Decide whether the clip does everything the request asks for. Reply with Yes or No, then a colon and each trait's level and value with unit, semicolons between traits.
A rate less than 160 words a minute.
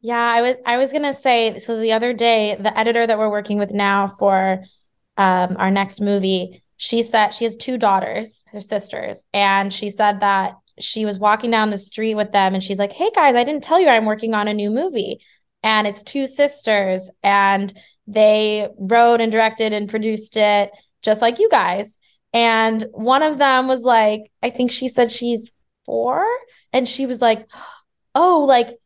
No: average, 195 wpm